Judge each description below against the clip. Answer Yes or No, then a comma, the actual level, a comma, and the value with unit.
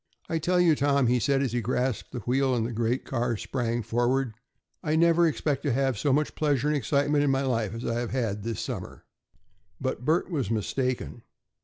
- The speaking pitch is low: Yes, low, 130 Hz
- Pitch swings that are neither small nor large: Yes, average, 3.5 semitones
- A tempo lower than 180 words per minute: No, fast, 205 wpm